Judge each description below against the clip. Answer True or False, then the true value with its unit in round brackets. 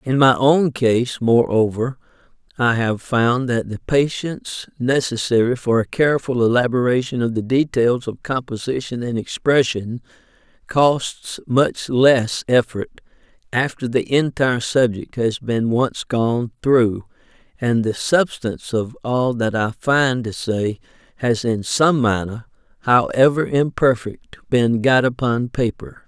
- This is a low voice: True (125 Hz)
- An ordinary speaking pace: False (130 wpm)